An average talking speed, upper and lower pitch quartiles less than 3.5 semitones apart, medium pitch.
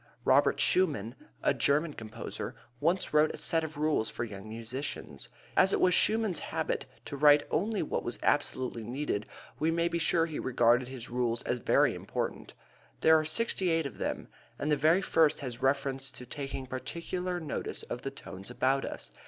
No: average, 180 wpm; average, 4.7 semitones; medium, 145 Hz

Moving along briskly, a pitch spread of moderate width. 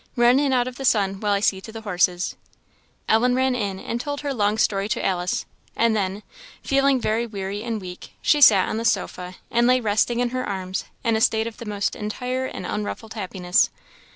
Yes: fast, 210 wpm; average, 3.8 semitones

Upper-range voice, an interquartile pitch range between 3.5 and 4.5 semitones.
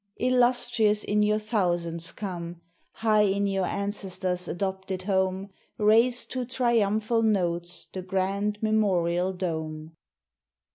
No: high, 195 Hz; average, 3.1 semitones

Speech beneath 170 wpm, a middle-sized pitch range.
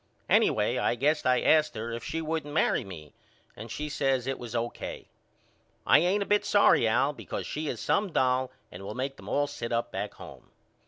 No: fast, 205 wpm; average, 4.4 semitones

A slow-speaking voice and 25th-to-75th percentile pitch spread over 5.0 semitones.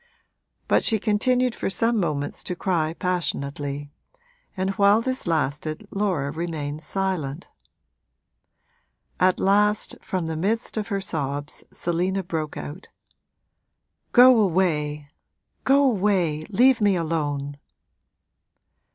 Yes: slow, 110 wpm; wide, 5.4 semitones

